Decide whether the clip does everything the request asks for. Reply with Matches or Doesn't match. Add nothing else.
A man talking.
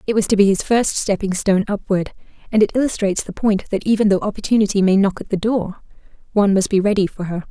Doesn't match